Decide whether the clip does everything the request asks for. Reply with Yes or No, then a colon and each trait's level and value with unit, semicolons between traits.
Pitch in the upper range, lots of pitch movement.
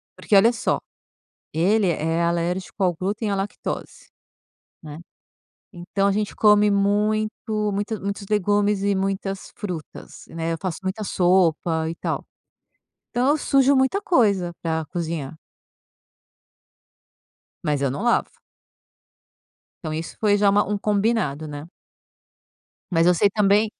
No: high, 195 Hz; average, 3.8 semitones